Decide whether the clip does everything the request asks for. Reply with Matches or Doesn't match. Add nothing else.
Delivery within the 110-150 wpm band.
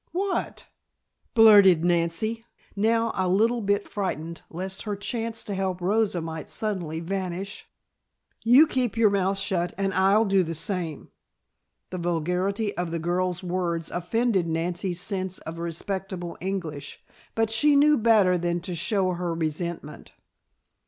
Matches